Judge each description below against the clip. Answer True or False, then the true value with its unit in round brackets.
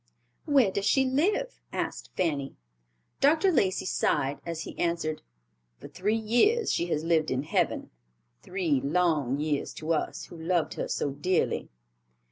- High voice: False (175 Hz)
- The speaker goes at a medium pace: True (145 wpm)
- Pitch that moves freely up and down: True (6.9 semitones)